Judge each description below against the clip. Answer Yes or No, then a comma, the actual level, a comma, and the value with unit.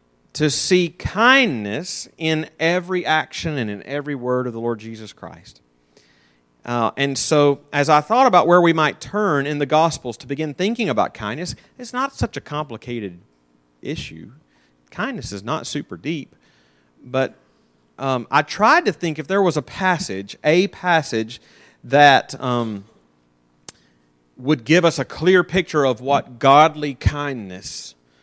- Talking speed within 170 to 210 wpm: No, average, 150 wpm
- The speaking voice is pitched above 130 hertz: Yes, medium, 140 Hz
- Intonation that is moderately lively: No, wide, 7.8 semitones